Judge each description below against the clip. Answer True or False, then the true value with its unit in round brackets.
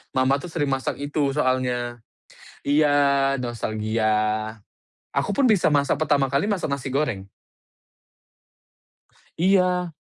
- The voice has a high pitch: False (140 Hz)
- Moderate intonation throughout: True (4.0 semitones)